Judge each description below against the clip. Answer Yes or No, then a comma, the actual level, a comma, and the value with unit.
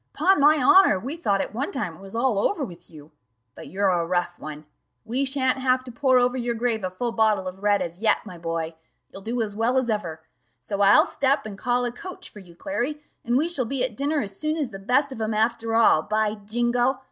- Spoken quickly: Yes, fast, 240 wpm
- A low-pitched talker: No, high, 230 Hz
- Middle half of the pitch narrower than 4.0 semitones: No, average, 4.9 semitones